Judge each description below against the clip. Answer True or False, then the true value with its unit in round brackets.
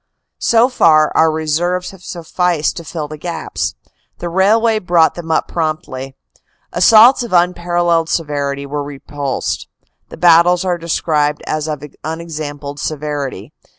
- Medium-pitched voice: True (160 Hz)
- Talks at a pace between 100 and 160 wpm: True (140 wpm)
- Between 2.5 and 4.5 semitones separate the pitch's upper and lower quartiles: True (3.0 semitones)